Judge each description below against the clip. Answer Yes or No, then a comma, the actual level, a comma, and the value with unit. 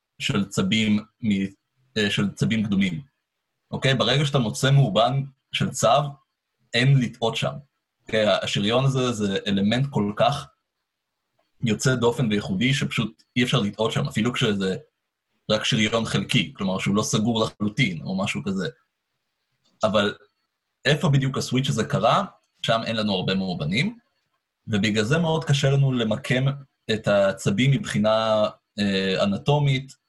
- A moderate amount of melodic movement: Yes, average, 4.6 semitones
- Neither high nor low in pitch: No, low, 120 Hz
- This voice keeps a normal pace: Yes, average, 130 wpm